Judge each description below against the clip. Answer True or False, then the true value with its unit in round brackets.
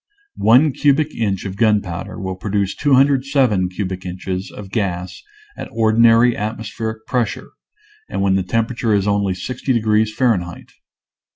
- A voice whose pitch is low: True (110 Hz)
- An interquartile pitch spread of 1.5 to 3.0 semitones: False (3.6 semitones)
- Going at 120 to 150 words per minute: True (135 wpm)